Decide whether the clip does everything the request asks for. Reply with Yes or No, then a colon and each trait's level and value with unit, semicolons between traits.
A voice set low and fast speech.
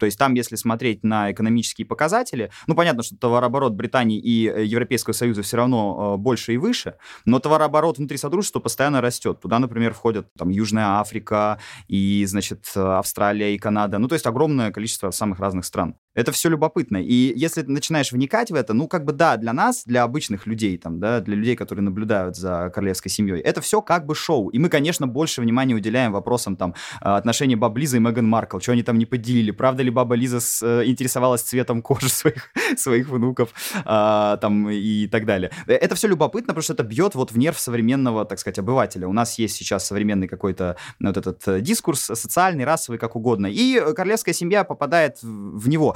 Yes: low, 120 Hz; fast, 190 wpm